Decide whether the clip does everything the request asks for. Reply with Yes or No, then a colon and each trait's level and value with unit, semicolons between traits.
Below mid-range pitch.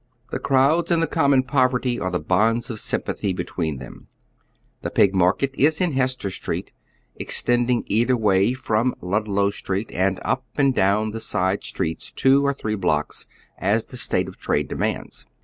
Yes: low, 110 Hz